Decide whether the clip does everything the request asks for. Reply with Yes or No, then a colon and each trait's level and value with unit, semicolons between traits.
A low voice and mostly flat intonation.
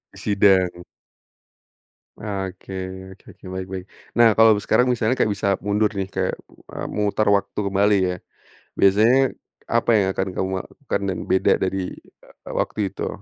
Yes: low, 100 Hz; narrow, 2.1 semitones